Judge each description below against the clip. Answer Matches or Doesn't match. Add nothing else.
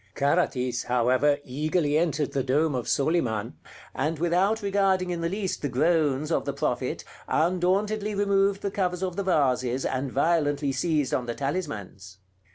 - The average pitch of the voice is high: Doesn't match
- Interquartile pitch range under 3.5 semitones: Doesn't match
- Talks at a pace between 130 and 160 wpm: Matches